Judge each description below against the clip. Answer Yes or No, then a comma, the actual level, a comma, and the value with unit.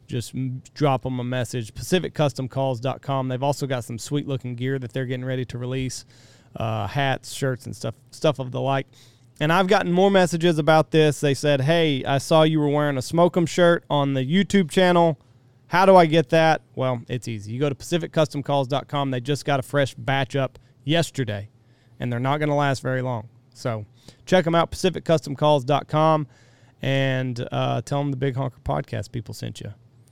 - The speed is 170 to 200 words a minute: Yes, average, 185 wpm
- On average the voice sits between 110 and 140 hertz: Yes, low, 135 Hz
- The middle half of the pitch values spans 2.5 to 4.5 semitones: Yes, average, 3.4 semitones